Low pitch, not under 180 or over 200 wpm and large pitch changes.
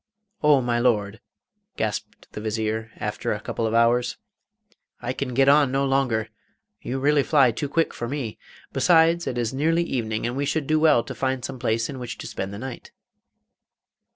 No: low, 125 Hz; average, 185 wpm; average, 3.6 semitones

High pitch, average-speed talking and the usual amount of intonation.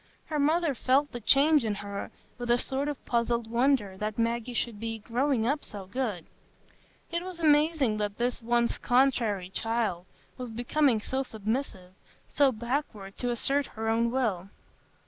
Yes: high, 240 Hz; average, 160 wpm; average, 3.9 semitones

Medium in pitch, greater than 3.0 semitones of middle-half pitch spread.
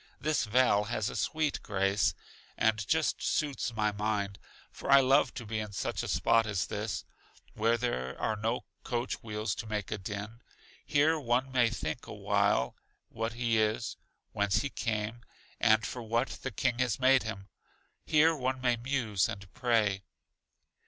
No: low, 115 Hz; average, 3.4 semitones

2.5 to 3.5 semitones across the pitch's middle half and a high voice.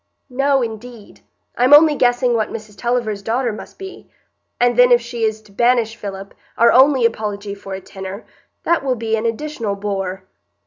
Yes: average, 3.1 semitones; high, 230 Hz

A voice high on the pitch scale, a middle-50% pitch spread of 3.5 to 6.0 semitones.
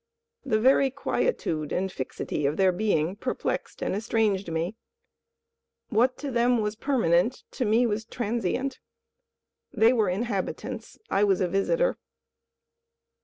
Yes: high, 215 Hz; average, 4.6 semitones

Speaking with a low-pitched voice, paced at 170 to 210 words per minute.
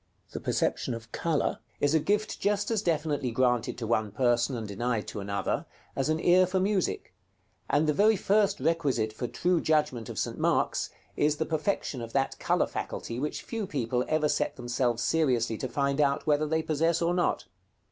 No: medium, 145 Hz; average, 190 wpm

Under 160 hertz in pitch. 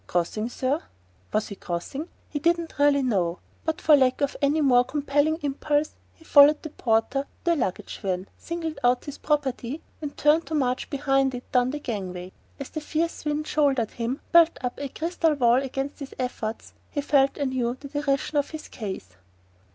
No: very high, 275 Hz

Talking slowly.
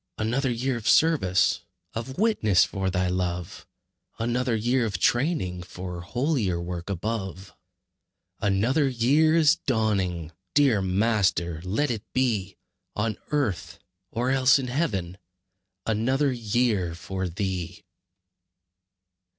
Yes: slow, 110 wpm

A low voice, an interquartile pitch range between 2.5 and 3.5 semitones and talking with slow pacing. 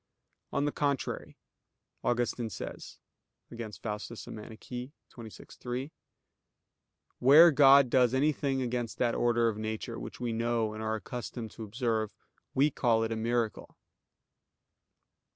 Yes: low, 120 Hz; average, 2.8 semitones; slow, 120 wpm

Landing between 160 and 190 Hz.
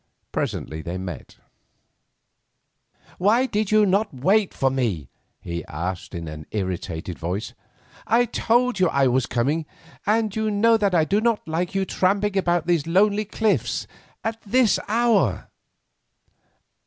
Yes: medium, 185 Hz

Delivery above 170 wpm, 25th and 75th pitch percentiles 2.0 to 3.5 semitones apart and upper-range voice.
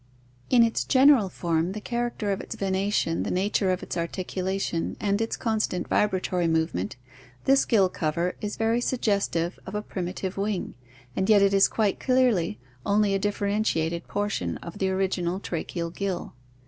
No: average, 160 wpm; average, 2.9 semitones; high, 195 Hz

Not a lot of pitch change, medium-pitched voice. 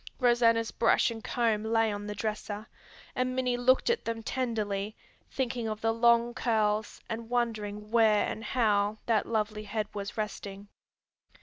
No: narrow, 2.0 semitones; high, 225 Hz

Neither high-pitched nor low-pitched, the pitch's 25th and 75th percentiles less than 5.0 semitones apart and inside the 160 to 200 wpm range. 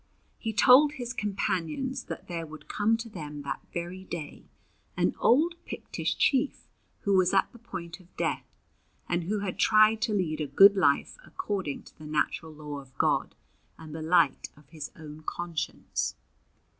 No: medium, 180 Hz; wide, 5.6 semitones; average, 170 wpm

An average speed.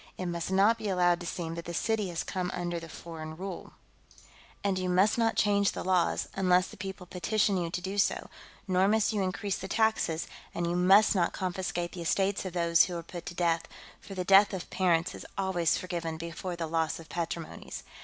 No: fast, 210 wpm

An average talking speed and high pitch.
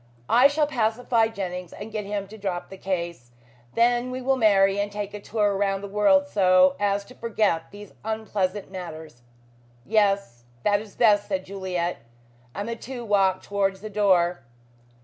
Yes: average, 170 wpm; high, 205 Hz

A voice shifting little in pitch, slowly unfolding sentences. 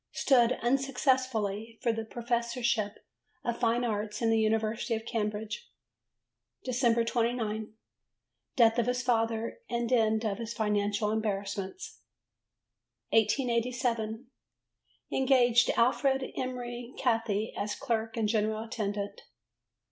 Yes: narrow, 2.0 semitones; slow, 105 wpm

